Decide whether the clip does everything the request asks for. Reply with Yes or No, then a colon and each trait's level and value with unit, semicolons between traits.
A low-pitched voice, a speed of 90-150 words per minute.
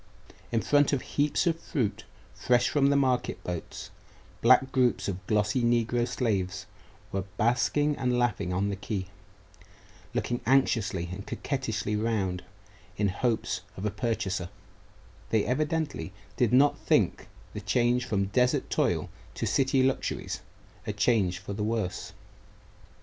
Yes: low, 115 Hz; slow, 135 wpm